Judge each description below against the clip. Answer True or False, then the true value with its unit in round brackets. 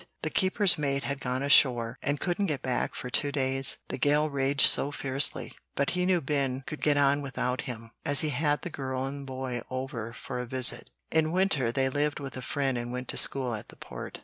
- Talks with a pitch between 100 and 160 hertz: True (135 Hz)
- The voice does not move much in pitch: True (2.2 semitones)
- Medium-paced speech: False (220 wpm)